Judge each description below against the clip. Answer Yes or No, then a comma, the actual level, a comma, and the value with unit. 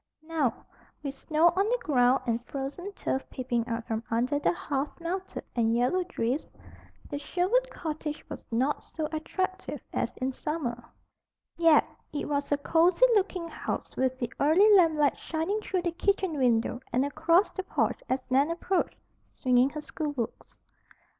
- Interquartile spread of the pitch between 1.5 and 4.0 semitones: No, average, 5.1 semitones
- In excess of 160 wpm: No, average, 155 wpm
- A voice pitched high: Yes, very high, 300 Hz